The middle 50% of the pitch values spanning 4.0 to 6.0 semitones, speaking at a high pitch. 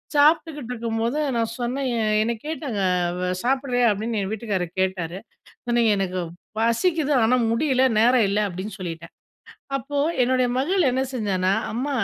Yes: average, 4.8 semitones; high, 235 Hz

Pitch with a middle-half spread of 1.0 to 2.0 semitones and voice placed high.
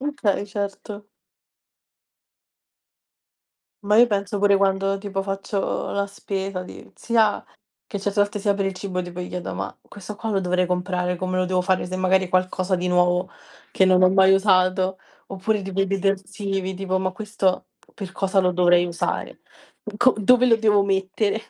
Yes: narrow, 1.6 semitones; high, 195 Hz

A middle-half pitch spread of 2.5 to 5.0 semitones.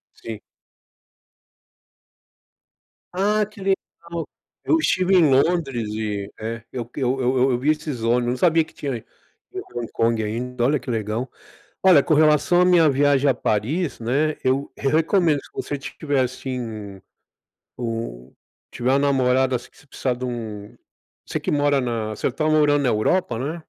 Yes: average, 4.6 semitones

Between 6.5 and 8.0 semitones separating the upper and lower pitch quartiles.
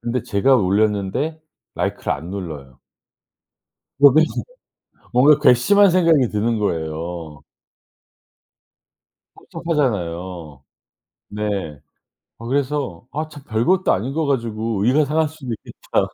Yes: wide, 7.6 semitones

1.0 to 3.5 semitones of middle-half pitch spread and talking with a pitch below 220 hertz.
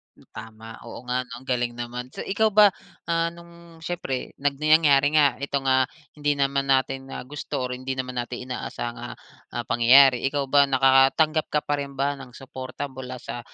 Yes: narrow, 2.5 semitones; low, 135 Hz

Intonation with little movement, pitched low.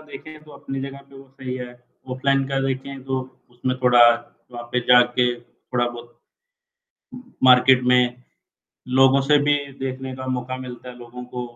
Yes: narrow, 1.5 semitones; low, 130 Hz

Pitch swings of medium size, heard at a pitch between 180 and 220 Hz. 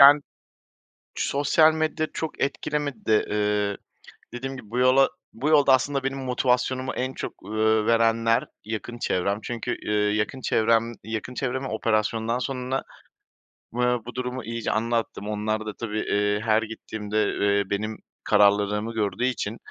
No: average, 3.3 semitones; low, 115 Hz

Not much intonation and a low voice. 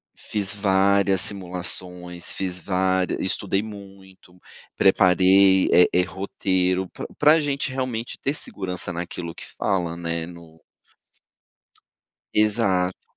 Yes: narrow, 1.8 semitones; very low, 95 Hz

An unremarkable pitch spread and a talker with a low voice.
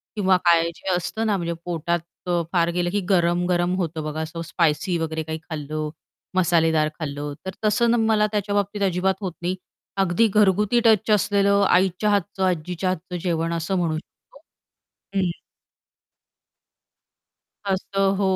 No: average, 3.1 semitones; medium, 180 Hz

